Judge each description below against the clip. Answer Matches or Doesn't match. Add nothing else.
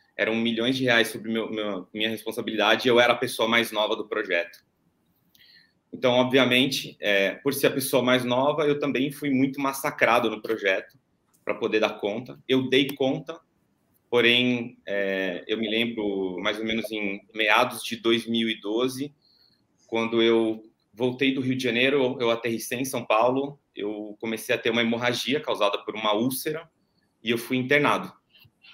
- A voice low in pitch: Matches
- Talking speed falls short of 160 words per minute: Doesn't match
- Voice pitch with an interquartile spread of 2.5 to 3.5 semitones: Matches